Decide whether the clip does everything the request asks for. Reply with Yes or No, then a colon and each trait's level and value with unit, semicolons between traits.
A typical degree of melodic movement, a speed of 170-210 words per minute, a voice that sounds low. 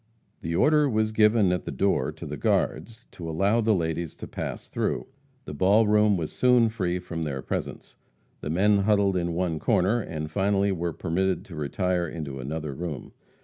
Yes: average, 4.4 semitones; average, 190 wpm; very low, 90 Hz